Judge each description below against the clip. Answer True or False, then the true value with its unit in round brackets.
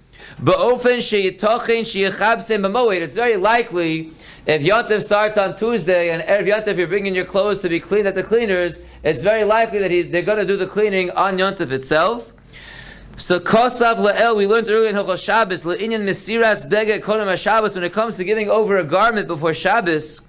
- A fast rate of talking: False (170 wpm)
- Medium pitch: False (200 Hz)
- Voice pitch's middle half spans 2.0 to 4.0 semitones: True (3.4 semitones)